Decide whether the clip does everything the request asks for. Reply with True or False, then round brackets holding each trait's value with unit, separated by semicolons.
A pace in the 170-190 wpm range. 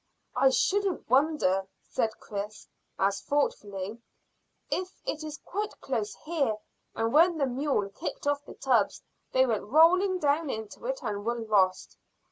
False (145 wpm)